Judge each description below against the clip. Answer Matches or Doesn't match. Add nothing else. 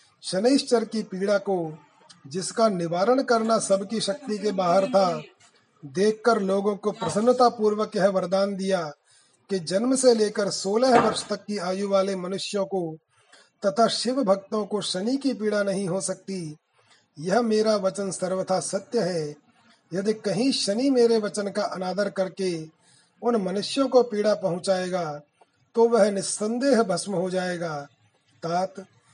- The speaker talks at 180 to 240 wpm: Doesn't match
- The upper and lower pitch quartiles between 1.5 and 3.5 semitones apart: Matches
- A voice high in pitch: Matches